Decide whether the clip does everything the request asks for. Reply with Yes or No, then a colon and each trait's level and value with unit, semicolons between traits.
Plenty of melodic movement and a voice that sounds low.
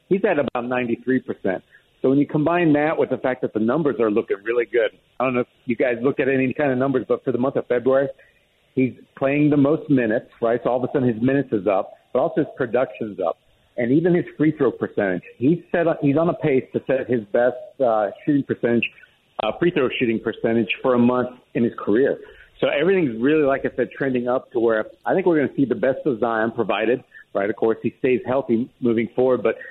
No: average, 3.6 semitones; low, 130 Hz